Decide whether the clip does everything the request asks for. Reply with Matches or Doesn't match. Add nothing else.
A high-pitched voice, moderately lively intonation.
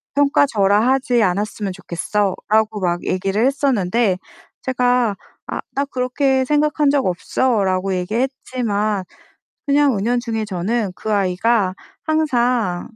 Matches